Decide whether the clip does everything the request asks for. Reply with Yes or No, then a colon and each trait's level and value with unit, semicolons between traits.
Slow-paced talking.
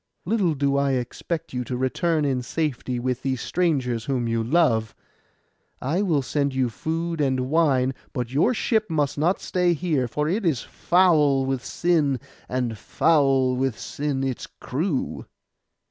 No: average, 155 wpm